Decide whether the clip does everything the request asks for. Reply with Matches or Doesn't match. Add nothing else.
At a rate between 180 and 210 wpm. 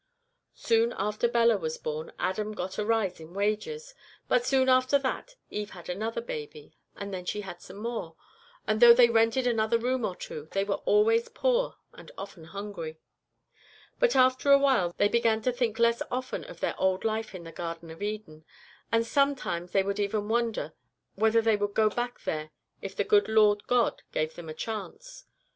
Matches